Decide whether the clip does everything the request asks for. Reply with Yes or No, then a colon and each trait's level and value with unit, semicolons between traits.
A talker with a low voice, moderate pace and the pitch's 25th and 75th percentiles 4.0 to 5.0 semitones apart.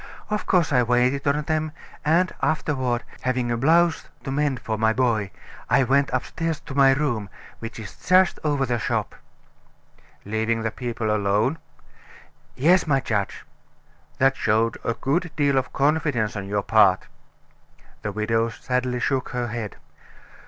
Yes: low, 130 Hz; average, 150 wpm; average, 4.5 semitones